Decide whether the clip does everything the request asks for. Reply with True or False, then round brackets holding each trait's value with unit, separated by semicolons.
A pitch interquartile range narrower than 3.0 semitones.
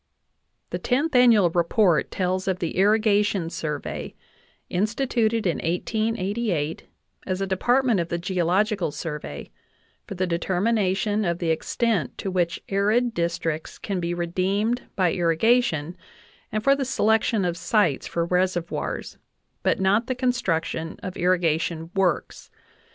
False (4.2 semitones)